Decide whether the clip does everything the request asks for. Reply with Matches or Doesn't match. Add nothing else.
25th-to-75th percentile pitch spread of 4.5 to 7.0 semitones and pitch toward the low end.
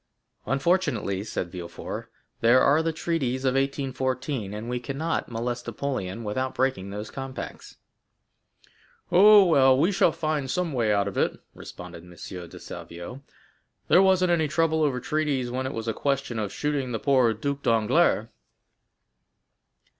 Matches